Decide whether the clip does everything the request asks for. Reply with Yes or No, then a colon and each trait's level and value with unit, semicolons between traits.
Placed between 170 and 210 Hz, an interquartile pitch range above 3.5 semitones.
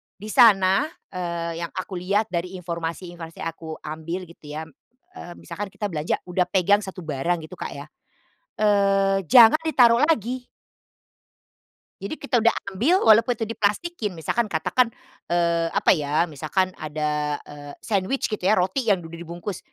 Yes: medium, 185 Hz; average, 4.2 semitones